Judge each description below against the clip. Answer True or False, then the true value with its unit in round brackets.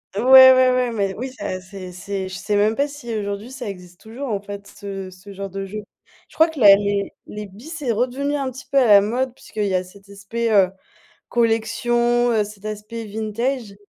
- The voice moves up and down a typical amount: True (3.5 semitones)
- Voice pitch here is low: False (215 Hz)